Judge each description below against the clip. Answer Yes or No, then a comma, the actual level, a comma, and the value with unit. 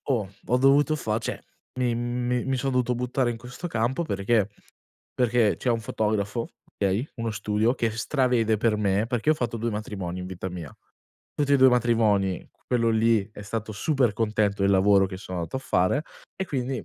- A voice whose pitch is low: Yes, low, 115 Hz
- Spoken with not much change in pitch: No, average, 3.3 semitones